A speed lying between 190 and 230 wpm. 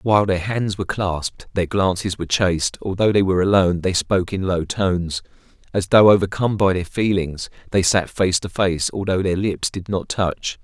Yes: average, 195 wpm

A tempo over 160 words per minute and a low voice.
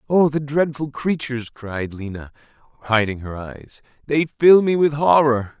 No: average, 150 wpm; low, 130 Hz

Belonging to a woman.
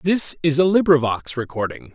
No: male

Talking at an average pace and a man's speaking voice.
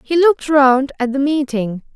No: average, 185 wpm; female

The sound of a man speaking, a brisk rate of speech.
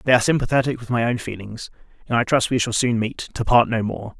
Yes: male; fast, 255 wpm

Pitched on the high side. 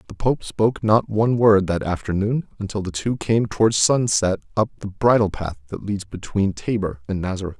No: low, 105 Hz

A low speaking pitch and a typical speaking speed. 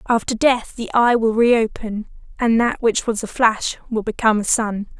No: high, 225 Hz; average, 190 wpm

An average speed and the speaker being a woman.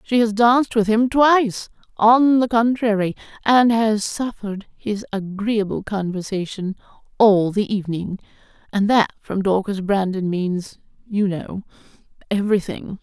No: slow, 125 wpm; female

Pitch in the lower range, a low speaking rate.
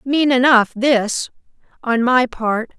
No: high, 245 Hz; slow, 130 wpm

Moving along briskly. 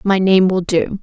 Yes: fast, 235 wpm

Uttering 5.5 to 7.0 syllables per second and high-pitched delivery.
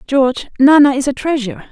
Yes: 6.3 syllables/s; very high, 275 Hz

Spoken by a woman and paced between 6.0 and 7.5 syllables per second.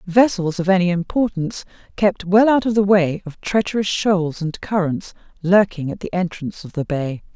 No: female; 5.0 syllables/s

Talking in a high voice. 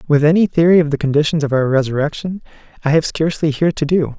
No: medium, 155 Hz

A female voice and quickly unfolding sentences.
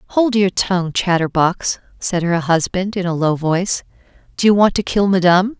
No: female; average, 180 wpm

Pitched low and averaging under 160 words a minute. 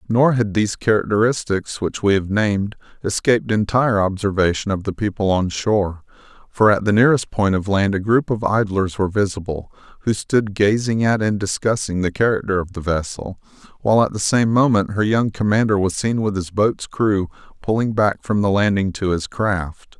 No: low, 100 Hz; average, 185 wpm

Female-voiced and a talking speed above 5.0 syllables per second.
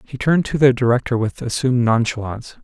No: male; 6.4 syllables/s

